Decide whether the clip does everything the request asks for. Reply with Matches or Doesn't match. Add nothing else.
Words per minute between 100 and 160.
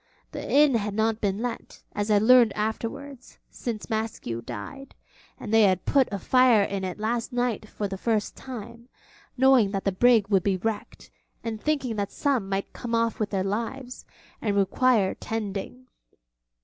Doesn't match